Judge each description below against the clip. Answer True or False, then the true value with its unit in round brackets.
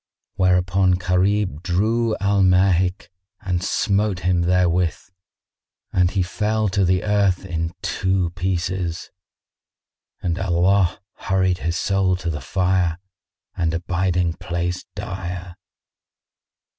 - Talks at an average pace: False (105 wpm)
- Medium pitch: False (90 Hz)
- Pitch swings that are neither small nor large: False (1.5 semitones)